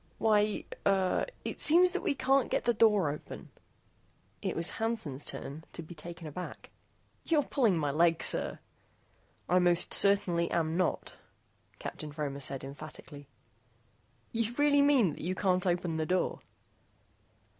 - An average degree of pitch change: No, wide, 6.0 semitones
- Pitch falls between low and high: Yes, medium, 180 Hz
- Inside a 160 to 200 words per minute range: No, average, 145 wpm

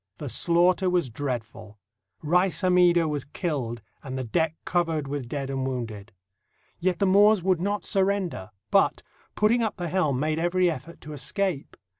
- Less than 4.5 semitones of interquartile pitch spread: No, average, 5.2 semitones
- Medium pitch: Yes, medium, 165 Hz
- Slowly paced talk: No, average, 160 wpm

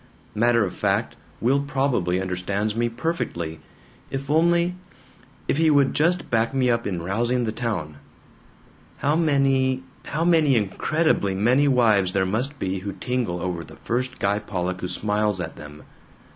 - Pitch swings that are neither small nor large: No, wide, 6.4 semitones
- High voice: No, low, 115 Hz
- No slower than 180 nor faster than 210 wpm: No, average, 150 wpm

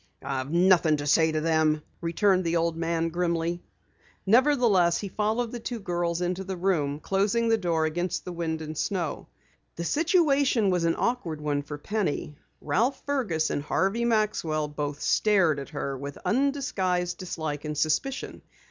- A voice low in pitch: No, medium, 175 Hz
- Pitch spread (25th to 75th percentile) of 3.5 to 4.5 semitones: No, average, 5.1 semitones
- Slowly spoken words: No, average, 160 wpm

